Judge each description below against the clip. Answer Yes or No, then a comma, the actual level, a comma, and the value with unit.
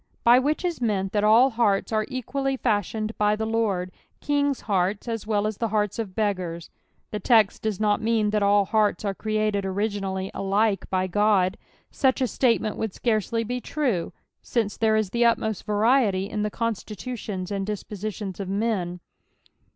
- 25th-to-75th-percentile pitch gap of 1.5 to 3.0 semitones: Yes, narrow, 2.5 semitones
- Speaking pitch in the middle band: No, high, 215 Hz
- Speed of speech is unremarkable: Yes, average, 165 wpm